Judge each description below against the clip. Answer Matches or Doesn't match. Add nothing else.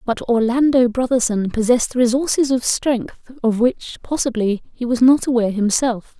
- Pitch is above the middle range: Matches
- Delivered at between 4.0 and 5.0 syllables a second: Matches